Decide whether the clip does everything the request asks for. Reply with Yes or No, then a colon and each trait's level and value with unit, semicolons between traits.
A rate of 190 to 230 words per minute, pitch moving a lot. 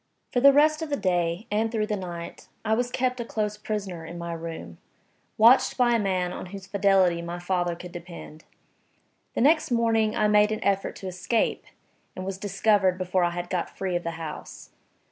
No: average, 200 wpm; average, 4.0 semitones